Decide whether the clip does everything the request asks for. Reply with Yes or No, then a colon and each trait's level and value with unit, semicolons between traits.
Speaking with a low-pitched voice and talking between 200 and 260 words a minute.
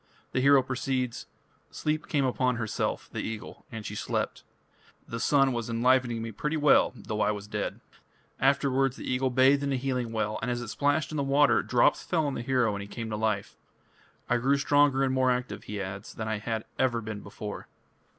Yes: low, 125 Hz; fast, 205 wpm